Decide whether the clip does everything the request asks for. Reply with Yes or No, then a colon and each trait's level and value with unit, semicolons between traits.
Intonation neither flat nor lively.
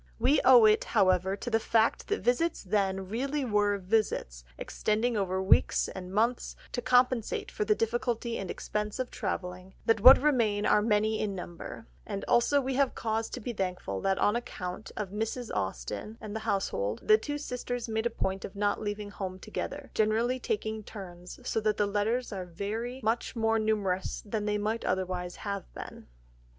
Yes: average, 3.5 semitones